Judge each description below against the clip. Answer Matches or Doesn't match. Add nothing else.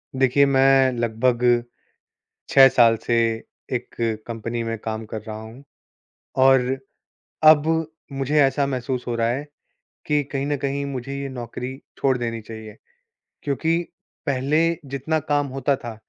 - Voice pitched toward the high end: Doesn't match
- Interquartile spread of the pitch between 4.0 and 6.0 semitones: Doesn't match